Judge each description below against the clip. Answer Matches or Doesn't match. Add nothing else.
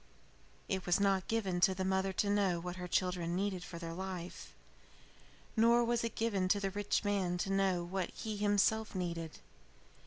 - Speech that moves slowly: Doesn't match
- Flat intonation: Matches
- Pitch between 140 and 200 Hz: Matches